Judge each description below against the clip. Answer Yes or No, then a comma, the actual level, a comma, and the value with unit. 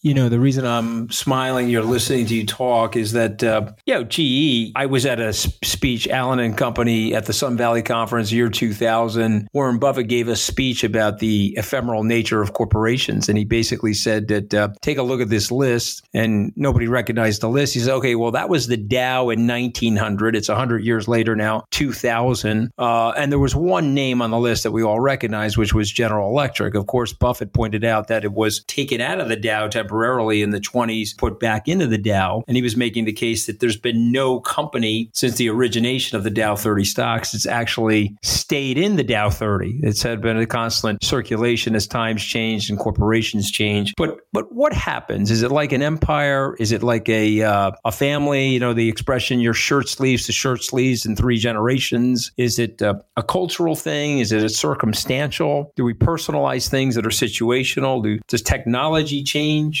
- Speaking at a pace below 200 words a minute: No, fast, 205 wpm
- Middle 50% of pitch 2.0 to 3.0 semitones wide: Yes, average, 2.7 semitones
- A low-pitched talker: Yes, low, 115 Hz